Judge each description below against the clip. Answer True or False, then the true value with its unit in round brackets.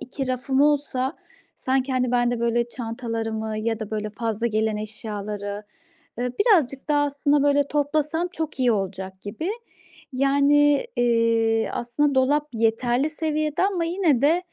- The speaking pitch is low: False (255 Hz)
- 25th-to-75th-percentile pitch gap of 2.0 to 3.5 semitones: False (4.6 semitones)